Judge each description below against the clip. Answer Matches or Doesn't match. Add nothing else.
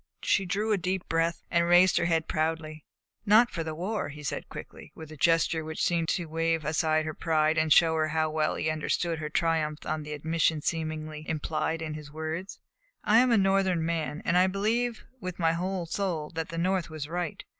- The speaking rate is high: Matches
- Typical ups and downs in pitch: Doesn't match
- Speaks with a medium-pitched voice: Matches